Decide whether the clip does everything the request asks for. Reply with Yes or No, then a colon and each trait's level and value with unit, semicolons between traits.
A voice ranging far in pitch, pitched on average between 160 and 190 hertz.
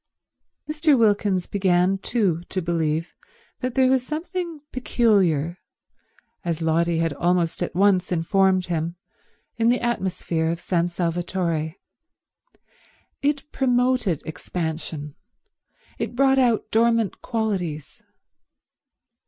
Yes: wide, 6.2 semitones; medium, 185 Hz